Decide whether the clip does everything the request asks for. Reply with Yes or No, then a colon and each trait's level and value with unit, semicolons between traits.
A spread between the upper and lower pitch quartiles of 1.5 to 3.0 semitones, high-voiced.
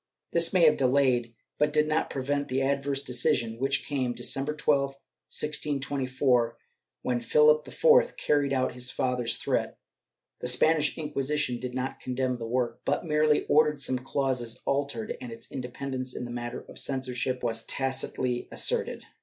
No: average, 2.7 semitones; low, 135 Hz